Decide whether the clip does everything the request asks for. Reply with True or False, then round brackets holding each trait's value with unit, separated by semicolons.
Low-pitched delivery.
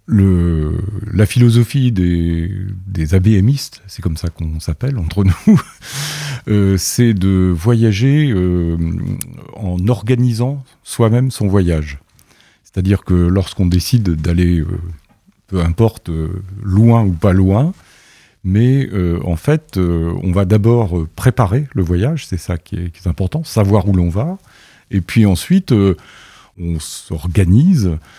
True (95 Hz)